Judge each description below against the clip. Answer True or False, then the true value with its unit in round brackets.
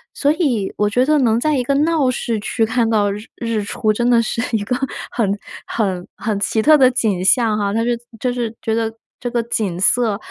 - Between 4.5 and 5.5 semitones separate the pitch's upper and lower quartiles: False (2.9 semitones)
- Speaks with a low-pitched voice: False (230 Hz)